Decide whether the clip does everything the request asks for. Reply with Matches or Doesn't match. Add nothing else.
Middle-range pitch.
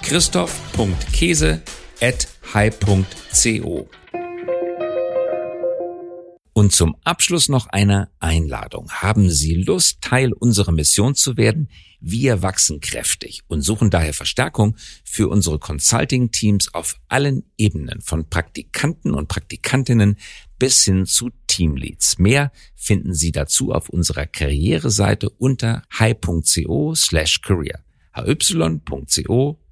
Doesn't match